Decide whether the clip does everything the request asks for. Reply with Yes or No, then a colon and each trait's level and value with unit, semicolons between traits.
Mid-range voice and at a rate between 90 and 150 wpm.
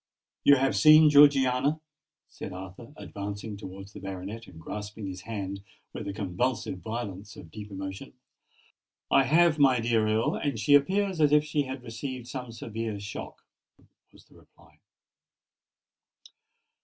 No: low, 115 Hz; average, 145 wpm